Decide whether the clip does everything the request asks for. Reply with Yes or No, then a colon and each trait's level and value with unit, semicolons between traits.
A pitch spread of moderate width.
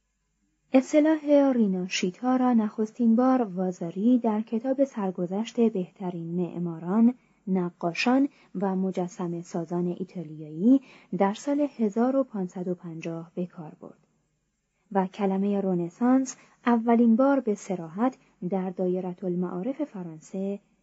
Yes: average, 4.9 semitones